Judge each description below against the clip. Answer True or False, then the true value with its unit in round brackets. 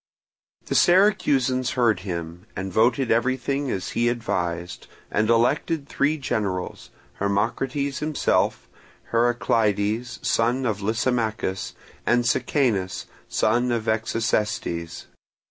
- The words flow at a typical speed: False (95 wpm)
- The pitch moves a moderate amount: True (4.1 semitones)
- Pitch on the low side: True (115 Hz)